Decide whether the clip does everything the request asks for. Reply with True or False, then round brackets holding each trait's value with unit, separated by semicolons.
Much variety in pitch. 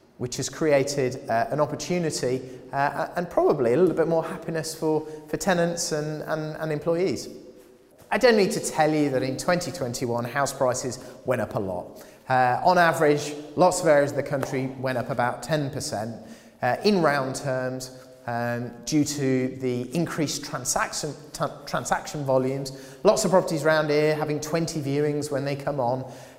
False (3.4 semitones)